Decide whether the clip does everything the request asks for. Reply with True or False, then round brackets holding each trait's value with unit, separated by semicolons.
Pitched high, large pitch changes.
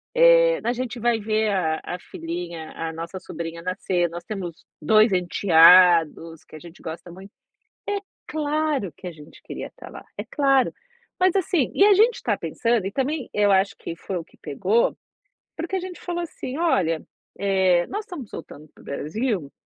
True (195 Hz; 8.4 semitones)